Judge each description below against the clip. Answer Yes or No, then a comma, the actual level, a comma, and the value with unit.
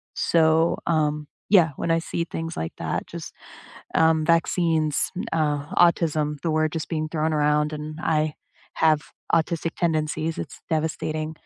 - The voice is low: No, medium, 155 Hz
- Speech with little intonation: Yes, narrow, 1.2 semitones